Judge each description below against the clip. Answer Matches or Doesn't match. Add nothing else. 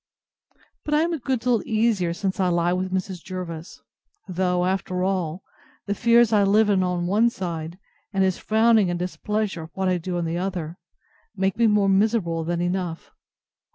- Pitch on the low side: Doesn't match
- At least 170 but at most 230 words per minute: Matches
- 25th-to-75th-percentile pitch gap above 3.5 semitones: Doesn't match